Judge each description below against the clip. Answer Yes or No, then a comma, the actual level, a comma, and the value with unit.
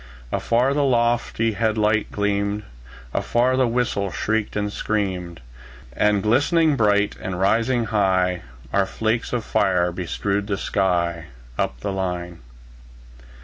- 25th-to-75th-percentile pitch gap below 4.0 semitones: Yes, average, 3.6 semitones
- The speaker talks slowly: Yes, slow, 125 wpm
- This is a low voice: Yes, low, 105 Hz